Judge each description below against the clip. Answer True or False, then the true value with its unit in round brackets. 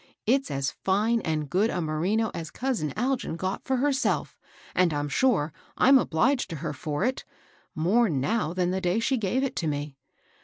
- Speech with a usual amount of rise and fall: False (7.8 semitones)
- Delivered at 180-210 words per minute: True (190 wpm)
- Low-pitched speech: False (185 Hz)